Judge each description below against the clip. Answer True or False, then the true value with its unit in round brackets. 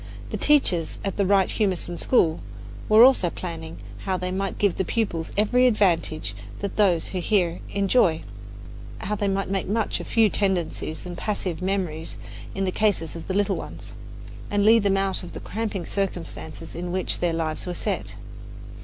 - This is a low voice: False (190 Hz)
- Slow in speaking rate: False (175 wpm)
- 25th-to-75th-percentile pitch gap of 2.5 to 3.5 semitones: True (2.9 semitones)